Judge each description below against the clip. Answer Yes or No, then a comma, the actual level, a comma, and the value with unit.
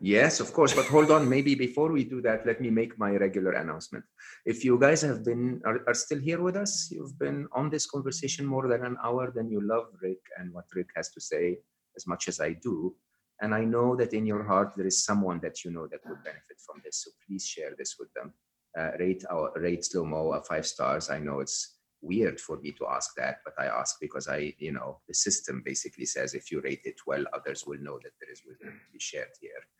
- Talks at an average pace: No, fast, 240 wpm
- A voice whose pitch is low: Yes, low, 125 Hz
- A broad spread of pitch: Yes, wide, 8.9 semitones